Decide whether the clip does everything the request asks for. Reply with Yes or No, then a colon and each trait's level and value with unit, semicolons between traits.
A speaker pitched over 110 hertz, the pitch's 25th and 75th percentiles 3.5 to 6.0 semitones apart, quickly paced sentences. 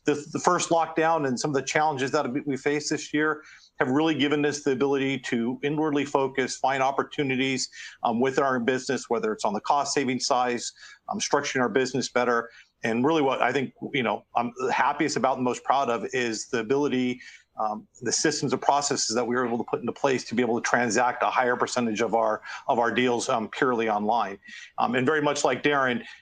No: low, 135 Hz; average, 2.8 semitones; fast, 215 wpm